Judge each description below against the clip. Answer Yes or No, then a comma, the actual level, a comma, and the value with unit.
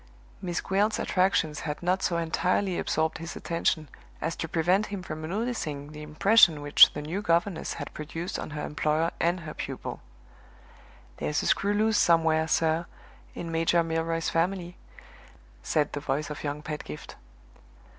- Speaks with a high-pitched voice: No, medium, 165 Hz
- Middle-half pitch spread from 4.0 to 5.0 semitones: No, average, 3.0 semitones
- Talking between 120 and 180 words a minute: Yes, average, 155 wpm